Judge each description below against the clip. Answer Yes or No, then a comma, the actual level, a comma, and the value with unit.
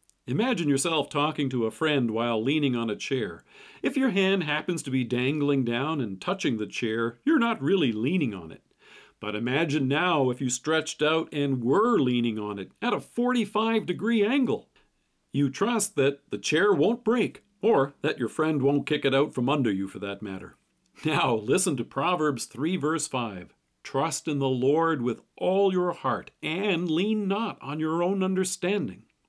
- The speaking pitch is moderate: Yes, medium, 150 Hz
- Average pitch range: No, wide, 5.8 semitones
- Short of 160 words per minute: No, average, 180 wpm